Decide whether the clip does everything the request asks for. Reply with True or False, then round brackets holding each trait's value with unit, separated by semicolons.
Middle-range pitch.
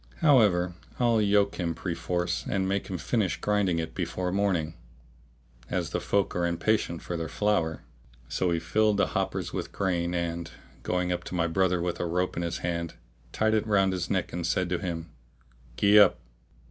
False (90 Hz)